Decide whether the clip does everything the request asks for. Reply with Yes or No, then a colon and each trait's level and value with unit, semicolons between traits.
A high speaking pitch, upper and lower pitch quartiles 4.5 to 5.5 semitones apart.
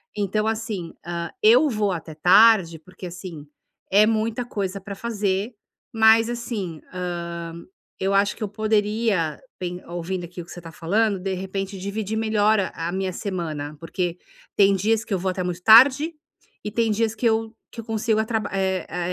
No: high, 195 Hz; average, 3.7 semitones